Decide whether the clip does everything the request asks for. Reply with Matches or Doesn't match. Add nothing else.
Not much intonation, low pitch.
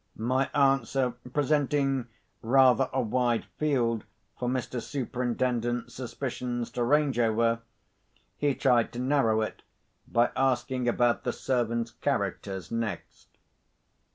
Matches